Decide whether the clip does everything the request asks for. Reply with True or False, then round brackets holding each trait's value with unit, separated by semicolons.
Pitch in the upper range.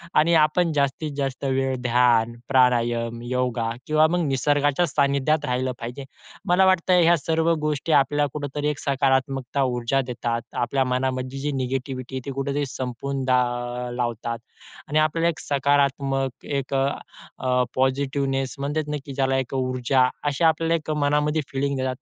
False (135 Hz)